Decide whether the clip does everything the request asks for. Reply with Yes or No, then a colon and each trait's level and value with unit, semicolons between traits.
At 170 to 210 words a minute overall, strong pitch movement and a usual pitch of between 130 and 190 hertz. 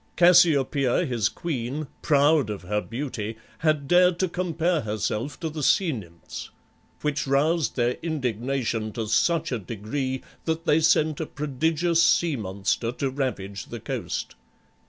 No: average, 140 wpm; wide, 5.9 semitones; medium, 140 Hz